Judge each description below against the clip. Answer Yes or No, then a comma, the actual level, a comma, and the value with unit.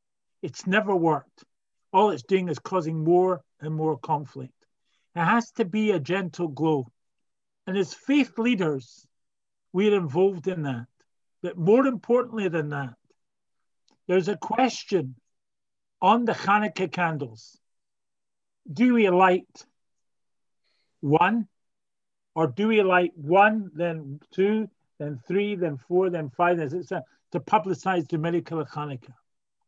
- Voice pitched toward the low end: No, medium, 175 Hz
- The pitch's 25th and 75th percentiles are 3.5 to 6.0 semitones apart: Yes, average, 4.9 semitones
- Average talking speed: No, slow, 130 wpm